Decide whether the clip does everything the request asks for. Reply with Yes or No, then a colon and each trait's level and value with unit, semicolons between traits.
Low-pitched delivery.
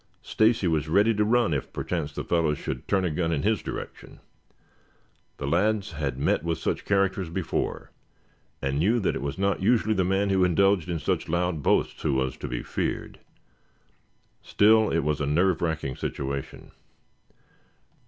Yes: very low, 85 Hz